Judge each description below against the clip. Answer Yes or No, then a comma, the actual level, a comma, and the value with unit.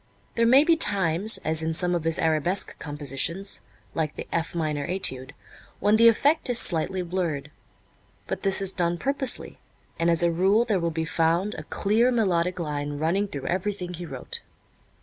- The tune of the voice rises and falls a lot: No, average, 4.1 semitones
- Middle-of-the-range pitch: Yes, medium, 175 Hz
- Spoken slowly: No, average, 175 wpm